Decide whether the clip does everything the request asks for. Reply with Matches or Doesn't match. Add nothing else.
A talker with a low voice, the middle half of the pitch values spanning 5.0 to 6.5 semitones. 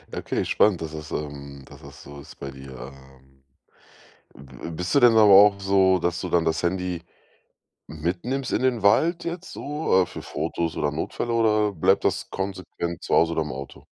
Matches